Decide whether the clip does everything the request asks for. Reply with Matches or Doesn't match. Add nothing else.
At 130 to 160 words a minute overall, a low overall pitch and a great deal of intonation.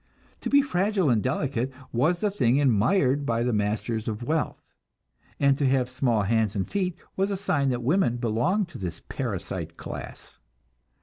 Doesn't match